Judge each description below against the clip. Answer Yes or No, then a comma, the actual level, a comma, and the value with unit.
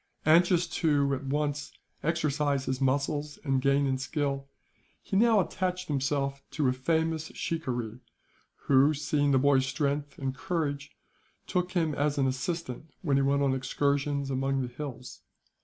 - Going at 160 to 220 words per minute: No, average, 150 wpm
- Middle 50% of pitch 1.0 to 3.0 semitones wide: Yes, narrow, 2.4 semitones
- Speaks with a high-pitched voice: No, medium, 140 Hz